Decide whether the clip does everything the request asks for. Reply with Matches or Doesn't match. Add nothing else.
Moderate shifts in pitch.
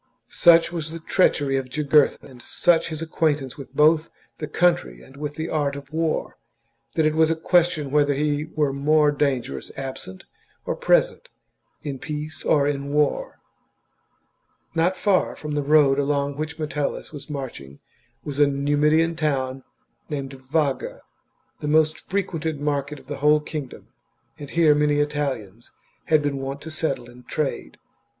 Doesn't match